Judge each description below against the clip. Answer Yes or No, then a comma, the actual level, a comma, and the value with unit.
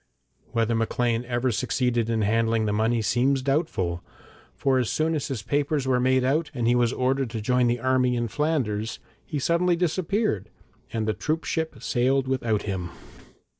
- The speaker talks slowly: No, average, 170 wpm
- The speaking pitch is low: Yes, low, 125 Hz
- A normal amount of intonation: Yes, average, 3.4 semitones